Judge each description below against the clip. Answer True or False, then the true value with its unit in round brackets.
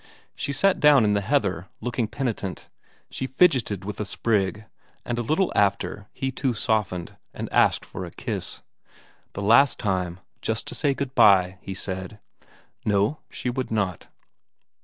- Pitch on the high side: False (110 Hz)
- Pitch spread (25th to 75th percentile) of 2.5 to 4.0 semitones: False (5.1 semitones)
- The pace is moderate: True (160 wpm)